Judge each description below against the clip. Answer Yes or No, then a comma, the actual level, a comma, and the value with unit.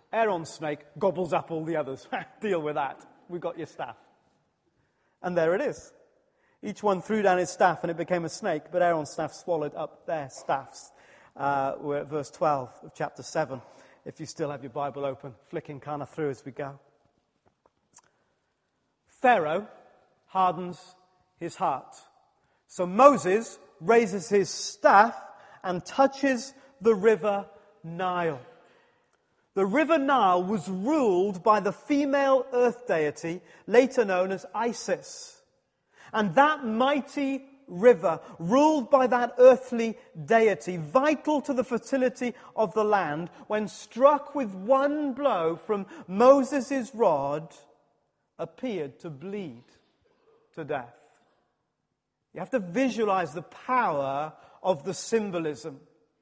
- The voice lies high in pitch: Yes, high, 195 Hz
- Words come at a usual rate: No, slow, 130 wpm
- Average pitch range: No, wide, 8.0 semitones